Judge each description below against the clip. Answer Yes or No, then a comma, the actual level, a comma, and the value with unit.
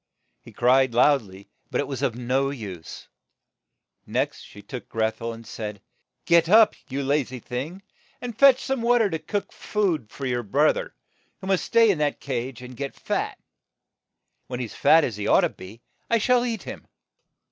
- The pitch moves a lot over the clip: Yes, wide, 8.5 semitones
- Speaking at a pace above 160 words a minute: Yes, average, 200 wpm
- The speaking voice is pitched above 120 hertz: Yes, low, 135 Hz